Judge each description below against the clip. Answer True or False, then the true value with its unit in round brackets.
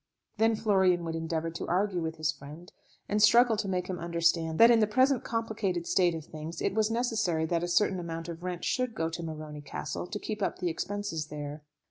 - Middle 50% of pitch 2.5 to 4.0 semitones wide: False (4.4 semitones)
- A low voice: False (175 Hz)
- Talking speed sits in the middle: False (215 wpm)